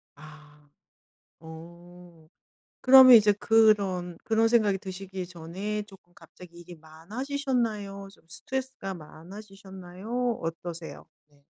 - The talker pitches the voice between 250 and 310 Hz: No, high, 190 Hz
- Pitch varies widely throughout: No, average, 4.1 semitones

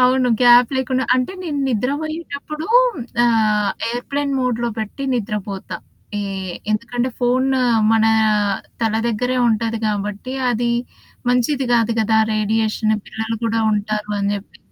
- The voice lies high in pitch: Yes, high, 235 Hz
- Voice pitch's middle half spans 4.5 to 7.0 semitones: No, average, 3.0 semitones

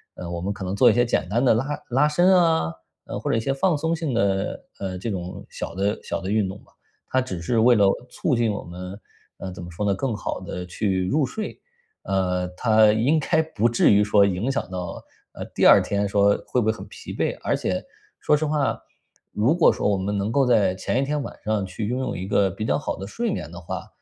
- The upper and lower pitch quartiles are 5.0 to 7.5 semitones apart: Yes, wide, 5.4 semitones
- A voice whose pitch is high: No, low, 105 Hz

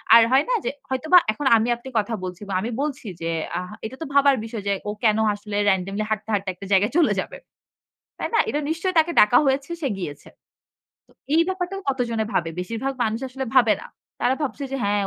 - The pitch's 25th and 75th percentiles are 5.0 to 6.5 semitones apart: Yes, wide, 5.4 semitones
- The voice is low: No, high, 235 Hz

